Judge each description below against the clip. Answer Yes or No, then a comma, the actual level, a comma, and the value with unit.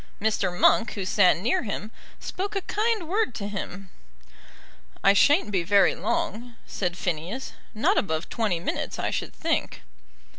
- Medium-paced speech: Yes, average, 150 wpm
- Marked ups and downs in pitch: Yes, wide, 5.7 semitones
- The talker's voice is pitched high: Yes, high, 205 Hz